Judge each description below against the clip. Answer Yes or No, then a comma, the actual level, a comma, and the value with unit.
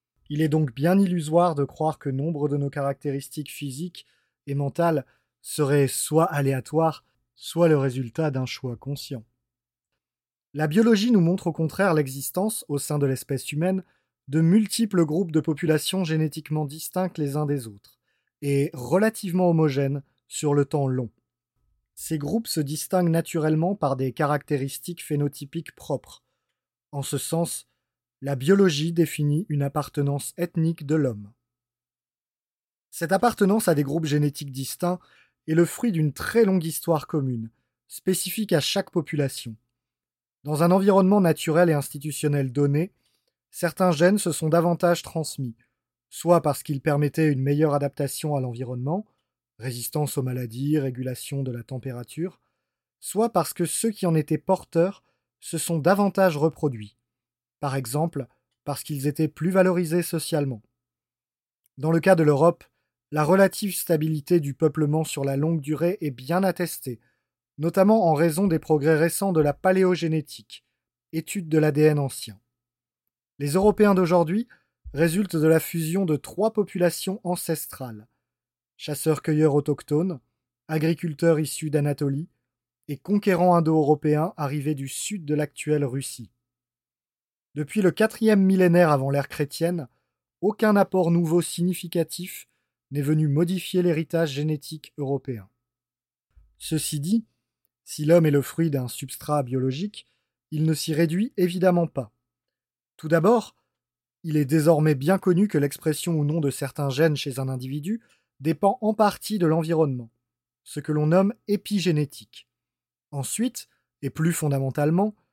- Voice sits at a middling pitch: Yes, medium, 155 Hz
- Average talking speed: No, slow, 135 wpm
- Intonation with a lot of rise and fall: No, average, 3.9 semitones